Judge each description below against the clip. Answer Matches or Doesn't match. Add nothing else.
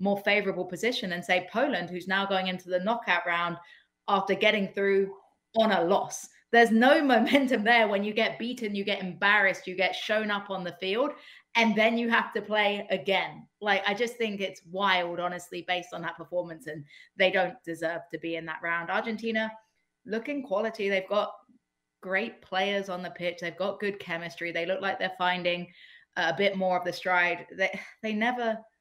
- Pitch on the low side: Doesn't match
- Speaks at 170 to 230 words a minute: Matches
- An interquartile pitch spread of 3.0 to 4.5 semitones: Matches